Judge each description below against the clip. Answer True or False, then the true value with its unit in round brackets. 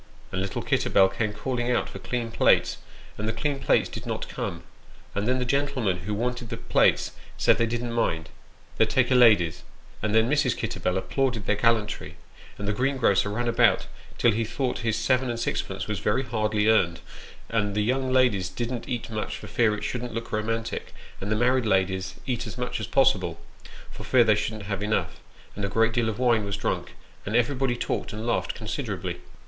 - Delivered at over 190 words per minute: True (200 wpm)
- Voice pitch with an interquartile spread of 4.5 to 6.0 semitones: False (3.0 semitones)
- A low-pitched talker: True (115 Hz)